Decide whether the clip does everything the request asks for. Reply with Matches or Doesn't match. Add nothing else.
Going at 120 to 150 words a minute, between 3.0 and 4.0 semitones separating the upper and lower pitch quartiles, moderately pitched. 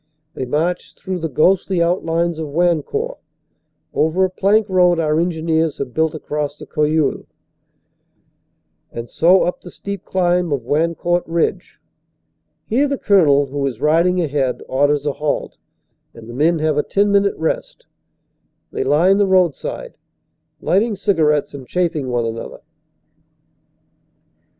Matches